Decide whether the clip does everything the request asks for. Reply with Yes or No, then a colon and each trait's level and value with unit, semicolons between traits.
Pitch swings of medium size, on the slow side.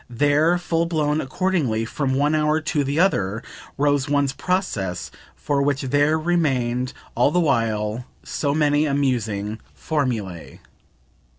Yes: average, 4.3 semitones; slow, 125 wpm